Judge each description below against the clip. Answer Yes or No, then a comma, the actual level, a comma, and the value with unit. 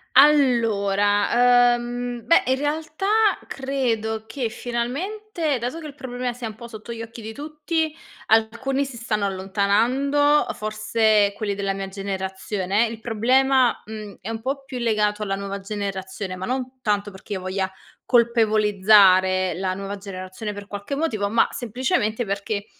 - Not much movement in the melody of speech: No, average, 4.1 semitones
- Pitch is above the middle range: Yes, high, 220 Hz